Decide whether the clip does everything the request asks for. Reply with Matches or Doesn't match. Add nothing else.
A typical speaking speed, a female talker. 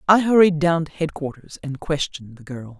Matches